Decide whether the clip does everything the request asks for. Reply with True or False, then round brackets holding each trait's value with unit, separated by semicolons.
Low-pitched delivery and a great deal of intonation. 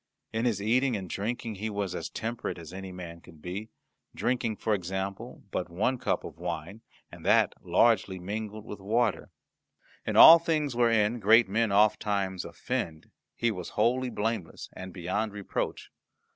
False (105 Hz; 3.5 semitones)